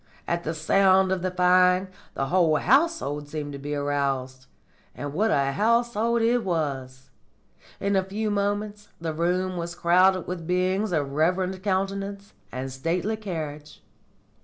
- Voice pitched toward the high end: No, medium, 180 Hz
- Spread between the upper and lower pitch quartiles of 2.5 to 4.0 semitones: No, average, 4.9 semitones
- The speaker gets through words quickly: No, average, 145 wpm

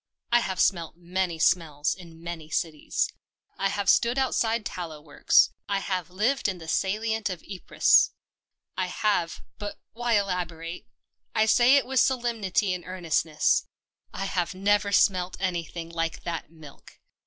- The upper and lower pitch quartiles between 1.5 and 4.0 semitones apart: Yes, average, 3.7 semitones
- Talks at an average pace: Yes, average, 150 wpm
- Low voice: No, medium, 185 Hz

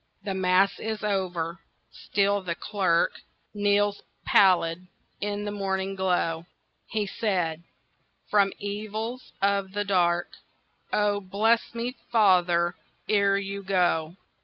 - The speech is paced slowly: Yes, slow, 110 wpm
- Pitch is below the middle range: No, high, 195 Hz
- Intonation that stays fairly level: Yes, narrow, 2.1 semitones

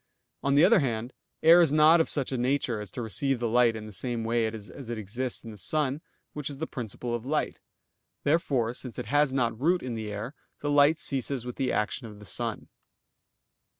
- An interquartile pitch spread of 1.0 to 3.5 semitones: No, average, 4.2 semitones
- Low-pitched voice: Yes, low, 125 Hz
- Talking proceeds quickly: Yes, fast, 215 wpm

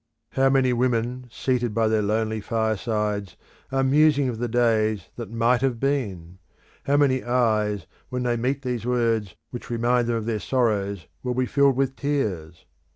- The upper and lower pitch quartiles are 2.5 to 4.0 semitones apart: Yes, average, 2.9 semitones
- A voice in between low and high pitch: No, low, 120 Hz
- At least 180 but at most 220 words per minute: No, average, 165 wpm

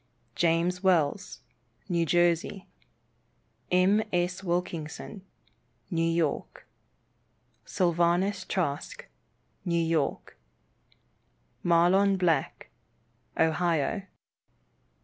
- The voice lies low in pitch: No, medium, 175 Hz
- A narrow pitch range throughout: Yes, narrow, 2.0 semitones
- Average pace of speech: No, slow, 65 wpm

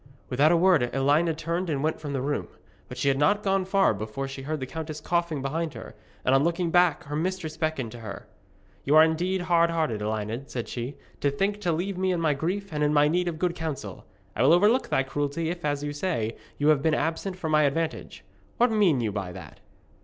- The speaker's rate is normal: No, fast, 230 wpm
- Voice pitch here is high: No, medium, 155 Hz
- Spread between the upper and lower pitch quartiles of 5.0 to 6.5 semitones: No, average, 4.1 semitones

